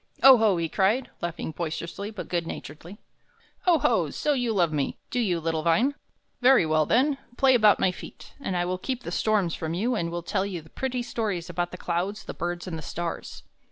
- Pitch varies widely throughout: Yes, wide, 5.7 semitones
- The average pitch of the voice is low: No, medium, 185 Hz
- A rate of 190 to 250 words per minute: Yes, average, 200 wpm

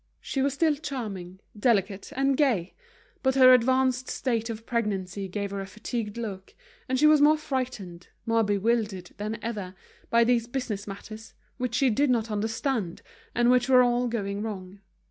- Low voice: No, high, 230 Hz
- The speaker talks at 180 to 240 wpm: No, average, 165 wpm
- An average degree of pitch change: Yes, average, 4.1 semitones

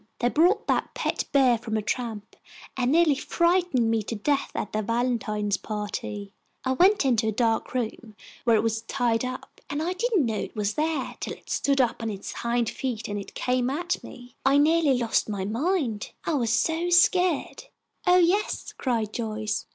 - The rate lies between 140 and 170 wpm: No, average, 180 wpm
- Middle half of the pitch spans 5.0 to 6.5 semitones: Yes, wide, 5.6 semitones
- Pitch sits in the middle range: No, high, 245 Hz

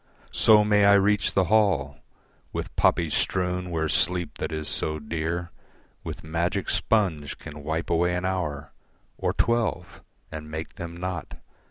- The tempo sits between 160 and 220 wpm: No, average, 150 wpm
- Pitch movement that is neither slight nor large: Yes, average, 3.4 semitones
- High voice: No, very low, 85 Hz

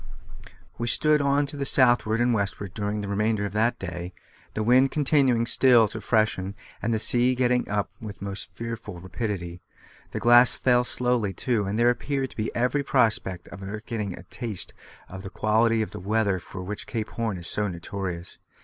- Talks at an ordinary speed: Yes, average, 190 wpm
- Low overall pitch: Yes, low, 110 Hz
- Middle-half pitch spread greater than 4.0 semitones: No, average, 3.6 semitones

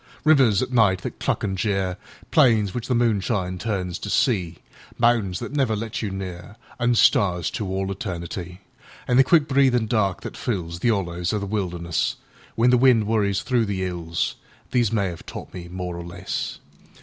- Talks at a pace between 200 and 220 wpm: No, average, 160 wpm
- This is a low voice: Yes, low, 100 Hz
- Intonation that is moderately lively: Yes, average, 4.5 semitones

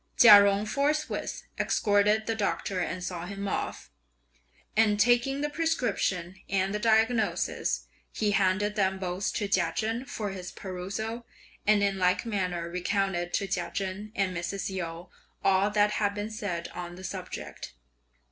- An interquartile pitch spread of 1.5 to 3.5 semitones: Yes, narrow, 2.6 semitones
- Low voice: No, high, 200 Hz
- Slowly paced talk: No, average, 150 wpm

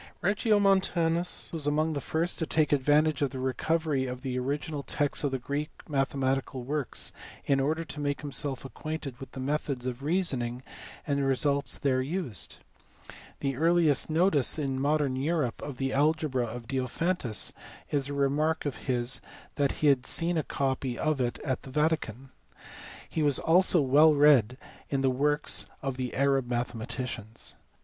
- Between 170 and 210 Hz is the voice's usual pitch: No, medium, 140 Hz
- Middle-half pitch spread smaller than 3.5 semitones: Yes, average, 2.9 semitones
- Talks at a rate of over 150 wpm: Yes, average, 160 wpm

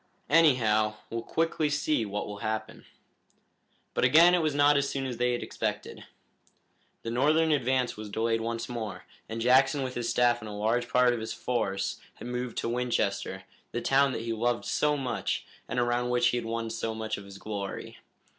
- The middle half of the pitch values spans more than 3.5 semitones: No, average, 3.0 semitones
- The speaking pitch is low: Yes, low, 120 Hz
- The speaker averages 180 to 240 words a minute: Yes, average, 195 wpm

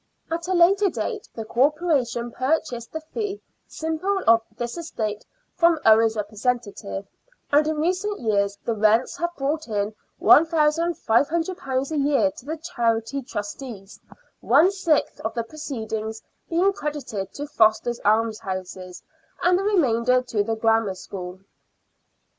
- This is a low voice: No, very high, 255 Hz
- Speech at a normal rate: No, slow, 130 wpm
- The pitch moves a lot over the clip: Yes, wide, 6.7 semitones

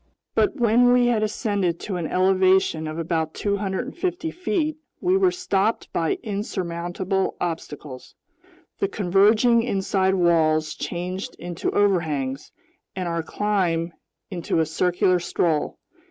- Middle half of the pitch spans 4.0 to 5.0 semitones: Yes, average, 4.3 semitones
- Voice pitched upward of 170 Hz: Yes, high, 190 Hz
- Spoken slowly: Yes, slow, 120 wpm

